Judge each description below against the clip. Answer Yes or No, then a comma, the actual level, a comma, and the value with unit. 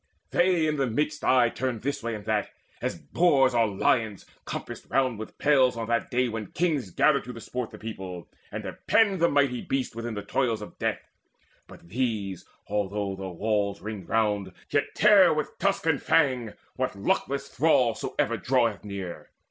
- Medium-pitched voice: No, low, 120 Hz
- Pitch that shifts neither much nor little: Yes, average, 5.0 semitones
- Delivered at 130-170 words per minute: No, average, 180 wpm